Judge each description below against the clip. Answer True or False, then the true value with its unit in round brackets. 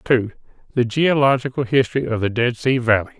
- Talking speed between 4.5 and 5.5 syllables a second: False (6.3 syllables/s)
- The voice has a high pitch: False (125 Hz)